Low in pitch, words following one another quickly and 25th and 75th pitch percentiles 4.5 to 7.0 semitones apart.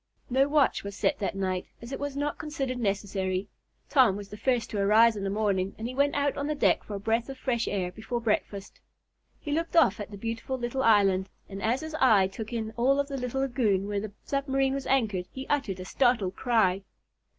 No: high, 230 Hz; fast, 225 wpm; average, 5.2 semitones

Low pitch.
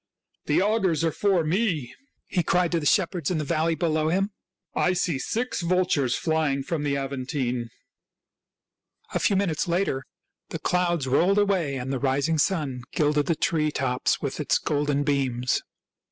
No: medium, 155 Hz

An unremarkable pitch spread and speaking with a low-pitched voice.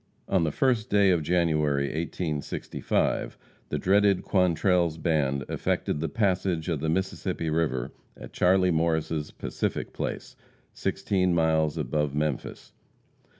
Yes: average, 3.2 semitones; very low, 80 Hz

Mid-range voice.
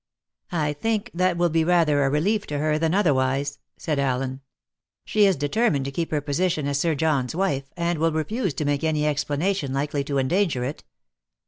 Yes: medium, 150 Hz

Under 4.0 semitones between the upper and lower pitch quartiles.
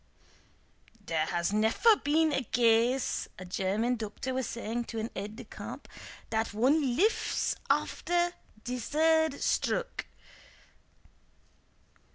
No: average, 5.1 semitones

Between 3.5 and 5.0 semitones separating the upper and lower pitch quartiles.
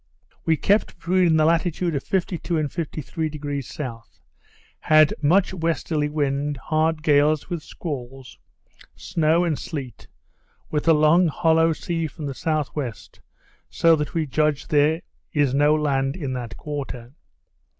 No: narrow, 2.4 semitones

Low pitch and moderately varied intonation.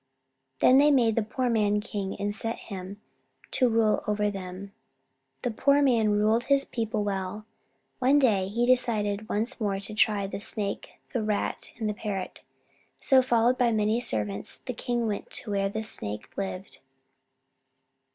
No: high, 215 Hz; average, 3.0 semitones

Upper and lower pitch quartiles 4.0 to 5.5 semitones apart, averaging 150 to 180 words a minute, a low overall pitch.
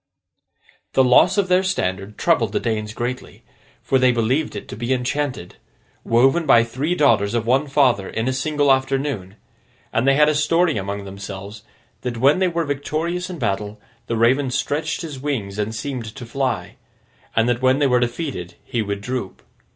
Yes: average, 4.8 semitones; average, 175 wpm; low, 130 Hz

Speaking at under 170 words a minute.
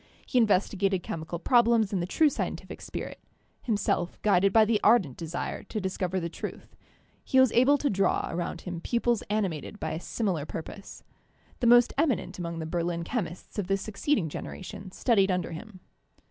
No: average, 175 wpm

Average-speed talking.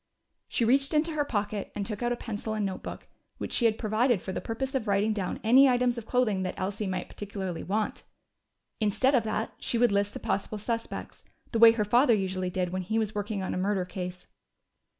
No: fast, 215 wpm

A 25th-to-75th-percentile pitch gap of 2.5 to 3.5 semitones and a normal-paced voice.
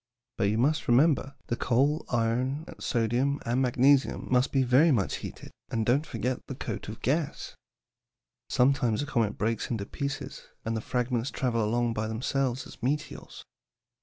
Yes: average, 3.1 semitones; average, 160 wpm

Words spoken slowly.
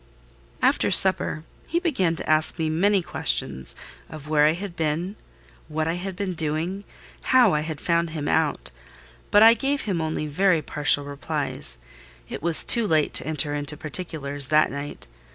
No: average, 170 wpm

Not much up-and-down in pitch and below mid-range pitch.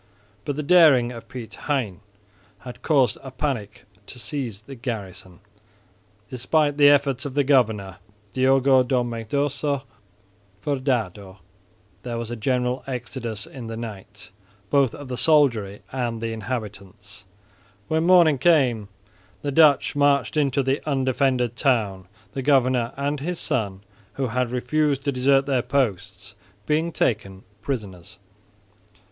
No: average, 3.9 semitones; low, 125 Hz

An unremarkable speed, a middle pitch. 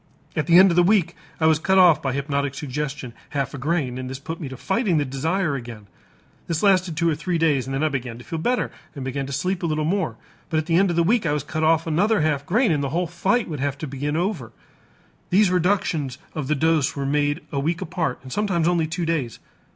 No: fast, 255 wpm; medium, 155 Hz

